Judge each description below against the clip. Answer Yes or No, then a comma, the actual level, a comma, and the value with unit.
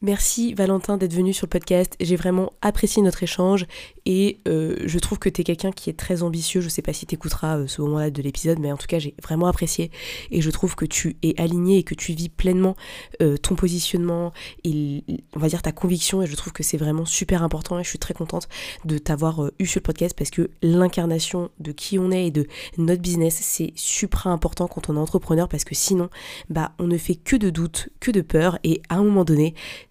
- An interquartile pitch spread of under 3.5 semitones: Yes, narrow, 2.6 semitones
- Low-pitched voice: No, medium, 175 Hz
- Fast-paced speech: Yes, fast, 240 wpm